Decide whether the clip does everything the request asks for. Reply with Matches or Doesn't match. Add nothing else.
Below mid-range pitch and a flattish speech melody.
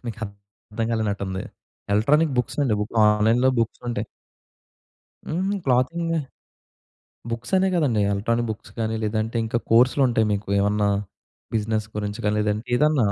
Doesn't match